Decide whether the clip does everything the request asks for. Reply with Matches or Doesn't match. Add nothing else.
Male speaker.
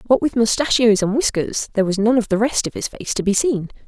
Doesn't match